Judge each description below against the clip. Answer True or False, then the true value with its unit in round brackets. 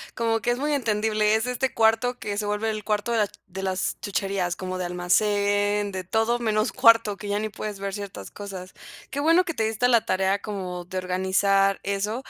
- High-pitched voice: True (205 Hz)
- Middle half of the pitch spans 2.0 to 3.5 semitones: True (2.5 semitones)